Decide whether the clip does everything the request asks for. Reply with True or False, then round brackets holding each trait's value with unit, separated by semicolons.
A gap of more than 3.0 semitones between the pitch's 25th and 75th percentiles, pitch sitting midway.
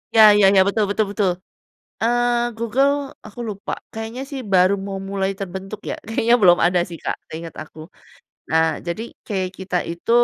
False (3.7 semitones; 200 Hz)